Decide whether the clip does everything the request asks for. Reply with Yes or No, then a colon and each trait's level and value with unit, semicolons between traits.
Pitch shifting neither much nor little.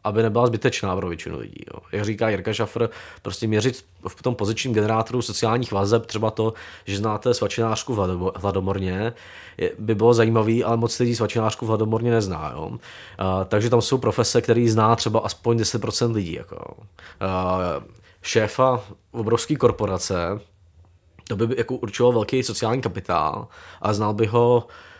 Yes: average, 3.0 semitones